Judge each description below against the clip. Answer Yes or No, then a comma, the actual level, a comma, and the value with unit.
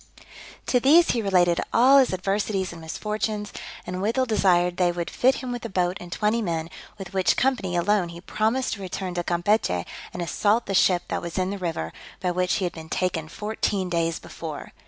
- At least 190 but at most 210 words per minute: Yes, average, 200 wpm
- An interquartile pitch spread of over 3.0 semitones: Yes, average, 3.6 semitones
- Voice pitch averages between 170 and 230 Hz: Yes, medium, 185 Hz